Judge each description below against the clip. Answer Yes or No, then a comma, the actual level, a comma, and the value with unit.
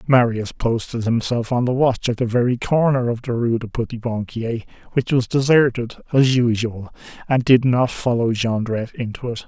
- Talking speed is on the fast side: No, average, 175 wpm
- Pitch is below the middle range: Yes, low, 120 Hz